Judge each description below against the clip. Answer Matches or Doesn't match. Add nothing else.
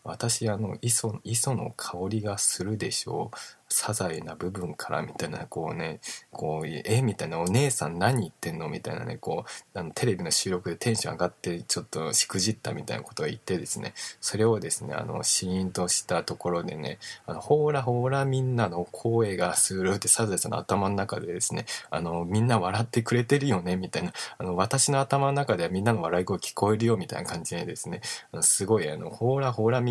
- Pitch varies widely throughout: Doesn't match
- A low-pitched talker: Matches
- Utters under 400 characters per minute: Doesn't match